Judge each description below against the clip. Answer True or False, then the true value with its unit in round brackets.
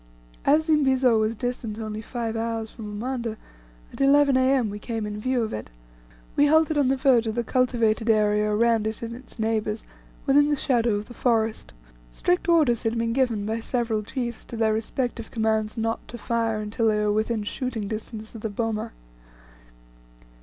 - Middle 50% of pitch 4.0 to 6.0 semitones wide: False (2.8 semitones)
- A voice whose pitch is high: True (230 Hz)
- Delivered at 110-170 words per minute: False (185 wpm)